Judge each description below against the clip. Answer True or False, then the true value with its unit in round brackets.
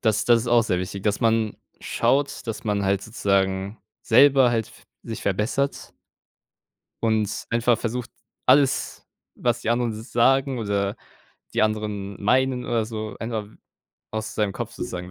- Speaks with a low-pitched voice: True (110 Hz)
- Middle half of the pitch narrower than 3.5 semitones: True (2.6 semitones)